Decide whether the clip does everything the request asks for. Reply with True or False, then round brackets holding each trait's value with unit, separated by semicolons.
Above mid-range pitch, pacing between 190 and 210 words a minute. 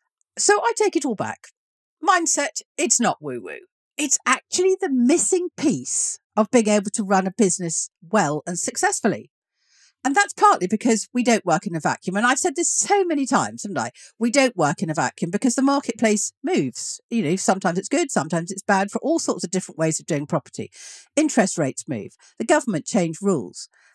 True (225 Hz; 195 wpm)